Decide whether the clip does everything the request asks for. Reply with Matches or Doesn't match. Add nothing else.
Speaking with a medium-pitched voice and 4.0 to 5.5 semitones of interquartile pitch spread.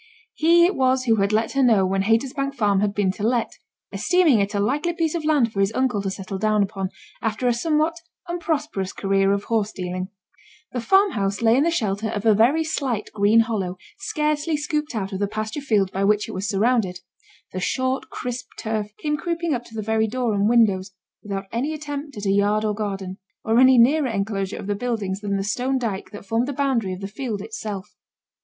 Doesn't match